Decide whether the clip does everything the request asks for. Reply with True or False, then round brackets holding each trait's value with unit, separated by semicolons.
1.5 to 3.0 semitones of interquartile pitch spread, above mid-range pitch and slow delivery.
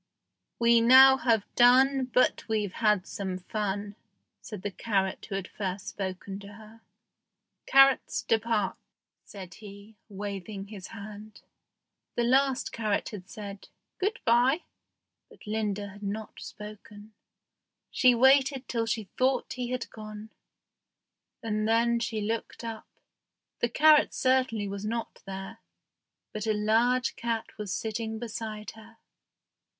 True (2.7 semitones; 220 Hz; 130 wpm)